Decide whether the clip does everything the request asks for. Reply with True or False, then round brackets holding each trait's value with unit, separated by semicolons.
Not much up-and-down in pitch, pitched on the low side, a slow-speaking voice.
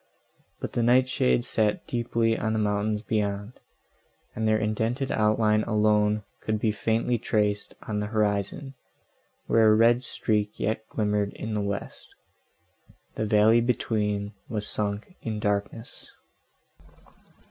True (1.4 semitones; 110 Hz; 130 wpm)